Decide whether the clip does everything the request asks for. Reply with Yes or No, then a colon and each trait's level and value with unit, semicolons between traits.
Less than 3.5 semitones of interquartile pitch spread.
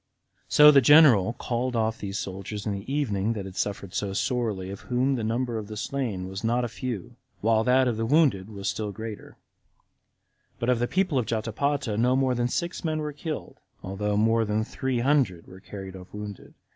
No: average, 4.1 semitones